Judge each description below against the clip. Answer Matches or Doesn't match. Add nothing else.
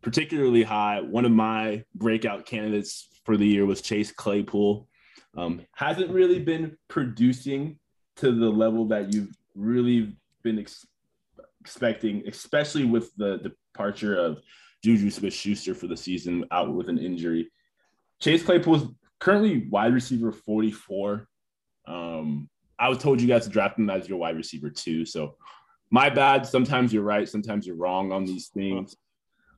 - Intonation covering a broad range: Doesn't match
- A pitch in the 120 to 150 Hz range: Doesn't match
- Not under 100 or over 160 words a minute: Matches